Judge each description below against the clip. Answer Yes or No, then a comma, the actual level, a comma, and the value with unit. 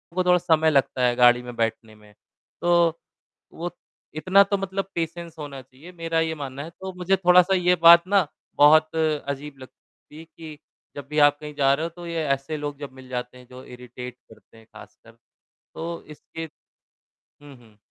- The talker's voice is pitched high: No, medium, 155 Hz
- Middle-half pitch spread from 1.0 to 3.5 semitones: No, average, 4.5 semitones